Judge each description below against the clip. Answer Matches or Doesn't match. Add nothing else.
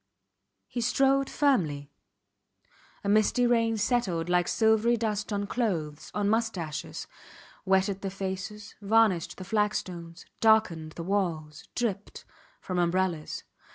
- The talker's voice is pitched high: Matches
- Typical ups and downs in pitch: Matches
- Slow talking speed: Matches